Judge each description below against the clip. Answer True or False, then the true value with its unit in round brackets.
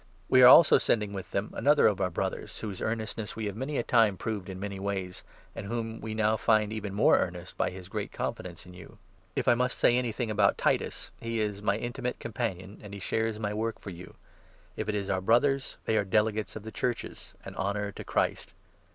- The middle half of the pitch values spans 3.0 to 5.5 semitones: False (2.4 semitones)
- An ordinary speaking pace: False (230 wpm)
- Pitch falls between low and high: False (105 Hz)